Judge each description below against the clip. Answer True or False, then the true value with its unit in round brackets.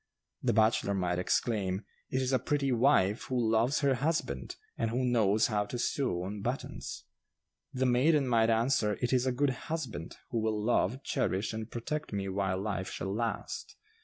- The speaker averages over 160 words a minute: True (175 wpm)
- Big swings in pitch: False (4.2 semitones)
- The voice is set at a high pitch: False (115 Hz)